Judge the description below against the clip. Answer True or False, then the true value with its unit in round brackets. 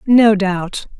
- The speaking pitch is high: True (205 Hz)